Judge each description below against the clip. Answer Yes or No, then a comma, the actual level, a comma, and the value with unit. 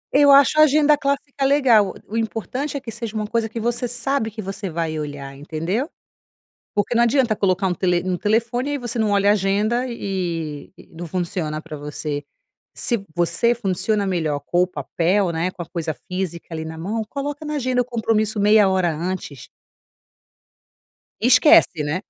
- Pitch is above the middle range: Yes, high, 205 Hz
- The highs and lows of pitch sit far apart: Yes, wide, 5.8 semitones